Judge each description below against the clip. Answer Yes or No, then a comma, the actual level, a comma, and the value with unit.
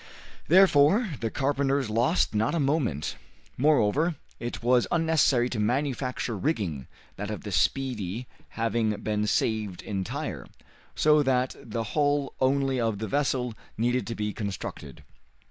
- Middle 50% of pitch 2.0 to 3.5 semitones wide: No, average, 4.9 semitones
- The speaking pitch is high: No, low, 125 Hz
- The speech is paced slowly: Yes, slow, 130 wpm